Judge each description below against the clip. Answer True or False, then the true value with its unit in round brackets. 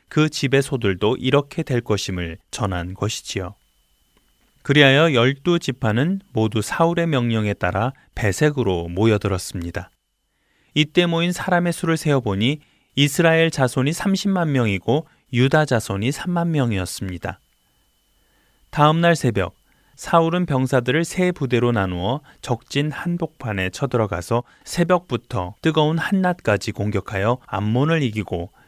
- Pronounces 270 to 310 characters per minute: True (285 characters per minute)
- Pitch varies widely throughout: True (7.6 semitones)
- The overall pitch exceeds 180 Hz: False (130 Hz)